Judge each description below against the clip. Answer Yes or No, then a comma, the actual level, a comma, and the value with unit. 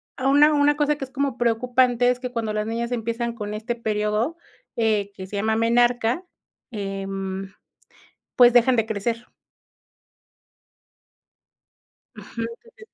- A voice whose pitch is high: Yes, high, 235 Hz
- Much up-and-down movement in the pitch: No, average, 2.8 semitones